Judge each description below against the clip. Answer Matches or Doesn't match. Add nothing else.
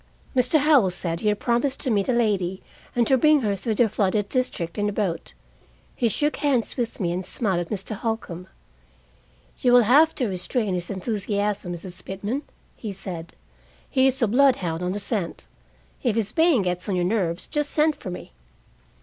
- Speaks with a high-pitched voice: Matches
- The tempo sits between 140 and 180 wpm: Doesn't match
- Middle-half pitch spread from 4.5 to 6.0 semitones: Matches